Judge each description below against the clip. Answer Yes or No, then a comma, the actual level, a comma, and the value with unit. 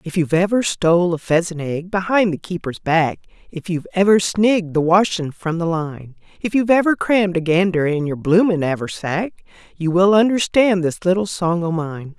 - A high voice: No, medium, 180 Hz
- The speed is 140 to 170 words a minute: No, average, 185 wpm